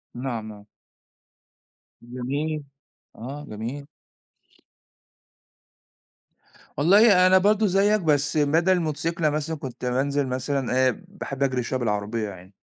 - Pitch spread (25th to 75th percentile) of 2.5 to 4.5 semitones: No, average, 4.9 semitones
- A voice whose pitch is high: No, medium, 140 Hz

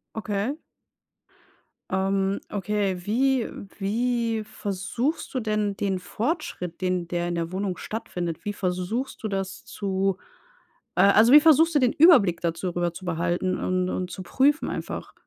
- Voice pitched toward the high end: Yes, high, 195 Hz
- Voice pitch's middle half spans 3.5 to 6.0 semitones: Yes, average, 4.1 semitones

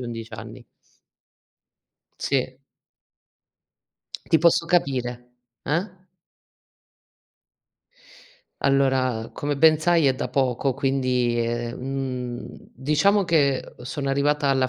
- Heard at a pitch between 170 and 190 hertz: No, low, 135 Hz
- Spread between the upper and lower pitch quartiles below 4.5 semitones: Yes, average, 2.9 semitones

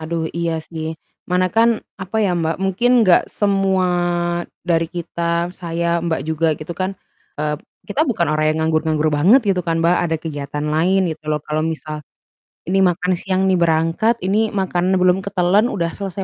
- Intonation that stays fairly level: No, average, 3.0 semitones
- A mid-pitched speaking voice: Yes, medium, 170 Hz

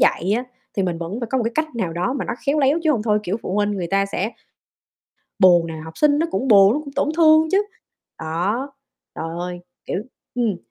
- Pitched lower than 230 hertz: Yes, high, 210 Hz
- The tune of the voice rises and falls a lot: Yes, wide, 7.3 semitones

